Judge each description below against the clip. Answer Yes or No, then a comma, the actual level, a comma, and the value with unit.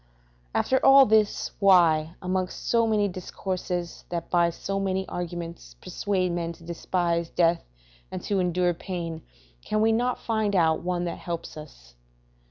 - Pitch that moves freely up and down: No, average, 2.7 semitones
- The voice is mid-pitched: Yes, medium, 180 Hz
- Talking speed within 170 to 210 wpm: No, average, 150 wpm